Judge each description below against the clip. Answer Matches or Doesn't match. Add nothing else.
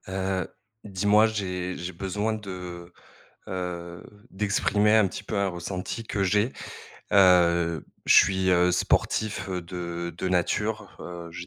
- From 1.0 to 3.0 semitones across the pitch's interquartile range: Matches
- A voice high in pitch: Doesn't match